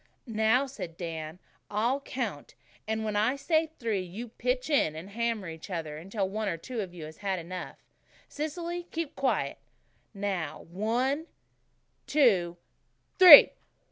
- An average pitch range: No, wide, 6.7 semitones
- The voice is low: No, high, 215 Hz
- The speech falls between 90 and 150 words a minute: Yes, slow, 135 wpm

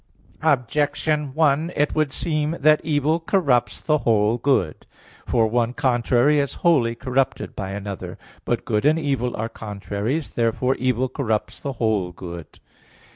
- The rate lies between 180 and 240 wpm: No, average, 140 wpm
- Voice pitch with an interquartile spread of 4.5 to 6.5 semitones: Yes, average, 4.9 semitones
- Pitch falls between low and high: No, low, 130 Hz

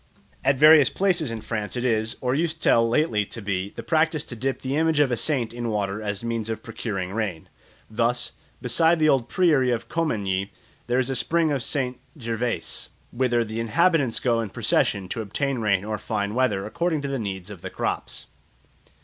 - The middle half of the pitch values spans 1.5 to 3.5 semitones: No, average, 4.8 semitones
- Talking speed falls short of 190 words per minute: No, average, 200 wpm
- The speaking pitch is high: No, low, 120 Hz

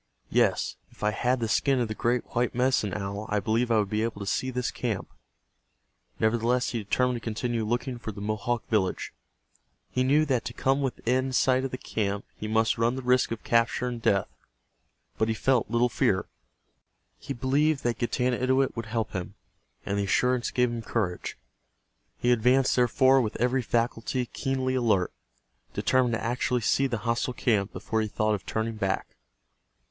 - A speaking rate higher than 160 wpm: Yes, average, 180 wpm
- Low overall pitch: Yes, low, 120 Hz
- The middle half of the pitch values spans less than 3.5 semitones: Yes, narrow, 2.6 semitones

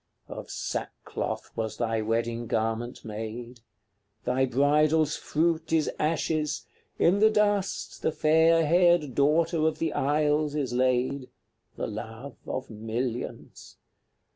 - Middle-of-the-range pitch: Yes, medium, 145 Hz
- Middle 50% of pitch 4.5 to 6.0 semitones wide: Yes, average, 5.0 semitones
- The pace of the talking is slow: Yes, slow, 120 wpm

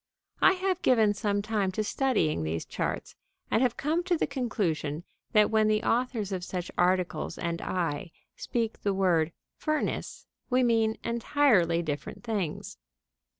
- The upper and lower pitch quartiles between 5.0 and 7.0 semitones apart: Yes, wide, 5.5 semitones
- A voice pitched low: No, high, 215 Hz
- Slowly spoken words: No, average, 150 wpm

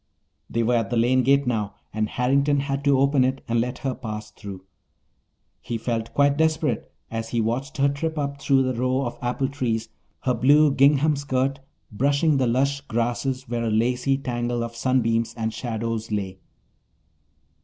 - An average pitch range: Yes, average, 3.2 semitones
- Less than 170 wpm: No, average, 175 wpm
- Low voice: Yes, low, 125 Hz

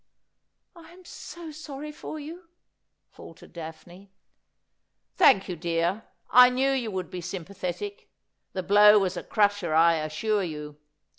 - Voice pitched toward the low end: No, high, 200 Hz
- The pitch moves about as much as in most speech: No, wide, 8.0 semitones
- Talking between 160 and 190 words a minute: No, average, 145 wpm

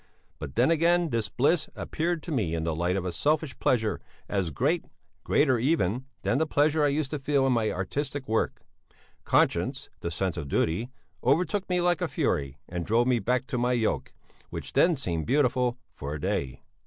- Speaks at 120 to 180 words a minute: No, average, 190 wpm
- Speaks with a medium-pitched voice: No, low, 125 Hz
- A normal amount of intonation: No, wide, 8.3 semitones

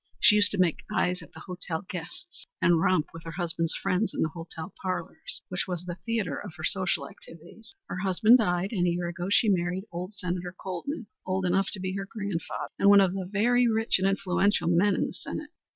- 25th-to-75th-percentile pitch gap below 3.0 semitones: Yes, narrow, 2.5 semitones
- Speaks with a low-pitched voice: No, medium, 185 Hz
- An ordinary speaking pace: No, fast, 215 wpm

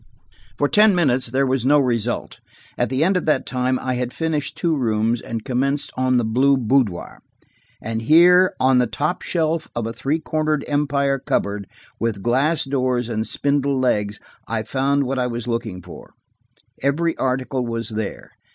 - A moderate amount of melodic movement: Yes, average, 3.6 semitones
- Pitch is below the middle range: Yes, low, 130 Hz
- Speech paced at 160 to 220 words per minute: Yes, average, 170 wpm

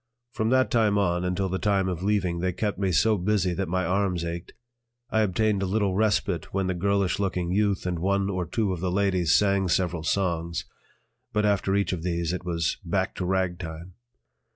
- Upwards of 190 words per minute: Yes, average, 200 wpm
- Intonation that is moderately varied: No, narrow, 2.3 semitones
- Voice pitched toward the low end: Yes, very low, 95 Hz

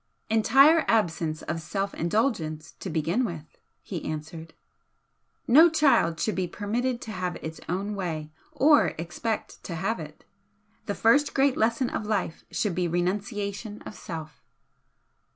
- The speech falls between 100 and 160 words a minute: Yes, average, 140 wpm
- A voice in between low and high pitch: No, high, 195 Hz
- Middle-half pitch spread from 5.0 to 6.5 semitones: Yes, wide, 5.6 semitones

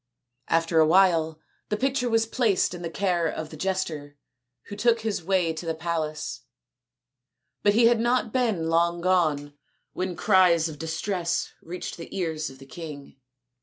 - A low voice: No, medium, 170 Hz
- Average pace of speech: Yes, average, 165 wpm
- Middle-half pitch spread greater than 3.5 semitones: Yes, average, 3.9 semitones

